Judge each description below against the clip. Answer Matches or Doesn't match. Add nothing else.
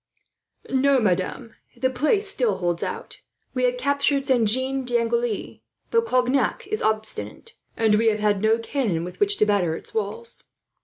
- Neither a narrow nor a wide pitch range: Matches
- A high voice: Matches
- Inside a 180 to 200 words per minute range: Doesn't match